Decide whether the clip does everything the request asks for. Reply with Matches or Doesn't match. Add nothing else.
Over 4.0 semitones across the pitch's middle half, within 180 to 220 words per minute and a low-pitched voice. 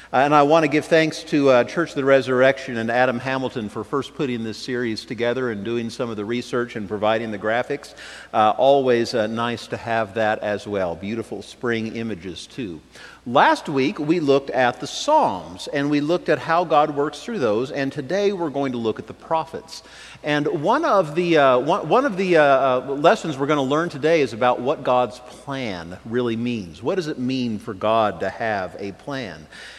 Matches